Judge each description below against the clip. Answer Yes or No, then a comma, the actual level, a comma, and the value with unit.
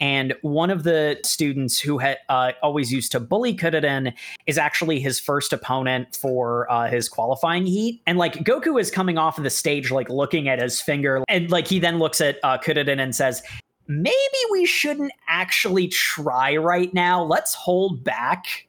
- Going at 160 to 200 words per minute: Yes, average, 185 wpm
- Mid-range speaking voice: Yes, medium, 150 Hz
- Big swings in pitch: No, average, 5.0 semitones